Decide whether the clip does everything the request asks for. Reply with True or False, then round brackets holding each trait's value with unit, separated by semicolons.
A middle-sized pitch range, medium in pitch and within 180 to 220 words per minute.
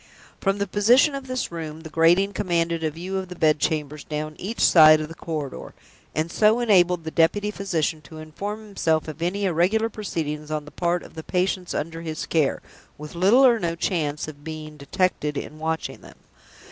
True (3.9 semitones; 165 Hz; 195 wpm)